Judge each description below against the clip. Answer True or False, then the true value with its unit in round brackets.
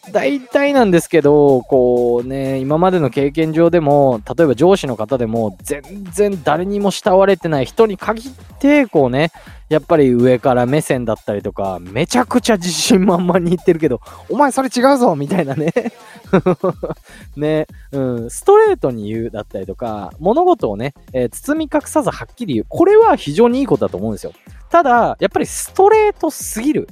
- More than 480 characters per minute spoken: False (350 characters per minute)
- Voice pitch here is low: False (175 Hz)